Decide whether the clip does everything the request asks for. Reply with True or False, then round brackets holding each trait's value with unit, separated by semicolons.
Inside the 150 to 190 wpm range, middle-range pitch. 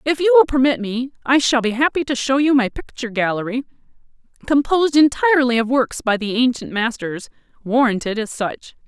False (170 wpm; 255 Hz)